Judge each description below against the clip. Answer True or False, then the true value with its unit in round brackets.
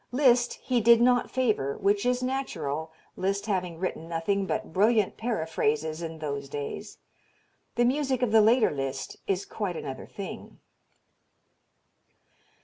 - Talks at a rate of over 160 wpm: False (135 wpm)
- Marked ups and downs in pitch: True (7.0 semitones)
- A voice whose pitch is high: True (200 Hz)